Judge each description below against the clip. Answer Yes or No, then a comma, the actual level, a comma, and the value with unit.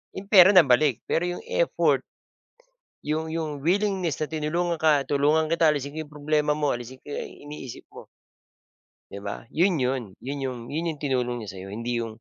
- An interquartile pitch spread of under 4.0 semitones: No, average, 4.3 semitones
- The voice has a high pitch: No, medium, 150 Hz